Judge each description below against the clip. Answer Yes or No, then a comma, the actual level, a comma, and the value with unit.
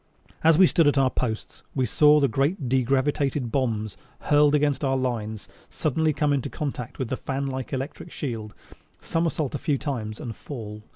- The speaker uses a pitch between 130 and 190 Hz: Yes, low, 135 Hz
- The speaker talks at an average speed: Yes, average, 175 wpm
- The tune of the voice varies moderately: Yes, average, 3.4 semitones